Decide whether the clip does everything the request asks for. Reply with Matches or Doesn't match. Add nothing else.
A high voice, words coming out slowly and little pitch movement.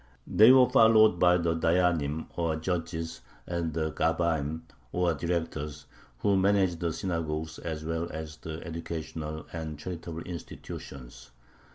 Doesn't match